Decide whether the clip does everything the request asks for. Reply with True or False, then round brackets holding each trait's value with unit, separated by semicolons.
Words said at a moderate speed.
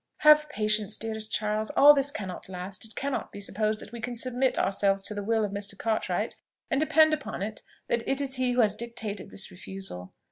False (210 wpm)